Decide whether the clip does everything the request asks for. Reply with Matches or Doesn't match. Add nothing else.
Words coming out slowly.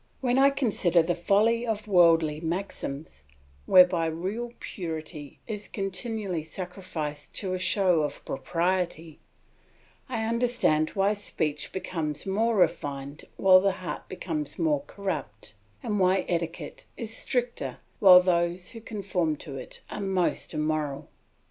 Matches